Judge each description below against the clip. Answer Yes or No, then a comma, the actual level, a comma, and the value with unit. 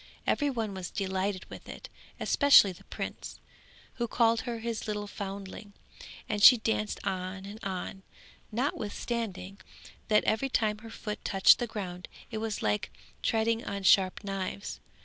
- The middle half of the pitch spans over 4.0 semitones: No, average, 2.7 semitones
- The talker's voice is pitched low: No, high, 210 Hz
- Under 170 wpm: Yes, average, 150 wpm